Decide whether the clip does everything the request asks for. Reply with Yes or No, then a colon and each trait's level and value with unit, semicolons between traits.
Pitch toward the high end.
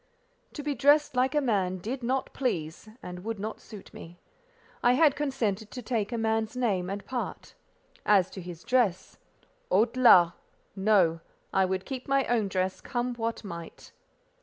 Yes: high, 220 Hz